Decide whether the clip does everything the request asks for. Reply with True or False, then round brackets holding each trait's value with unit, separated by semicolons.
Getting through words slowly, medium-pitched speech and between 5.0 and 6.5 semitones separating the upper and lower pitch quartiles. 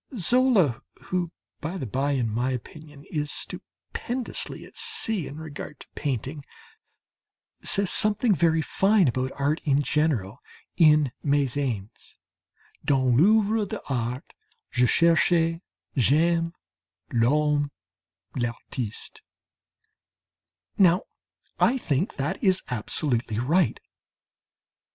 True (100 wpm; 150 Hz; 5.3 semitones)